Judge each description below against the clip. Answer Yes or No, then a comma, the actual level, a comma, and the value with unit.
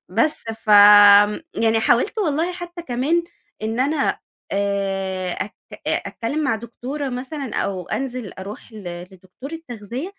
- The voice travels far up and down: Yes, wide, 5.9 semitones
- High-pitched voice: Yes, high, 230 Hz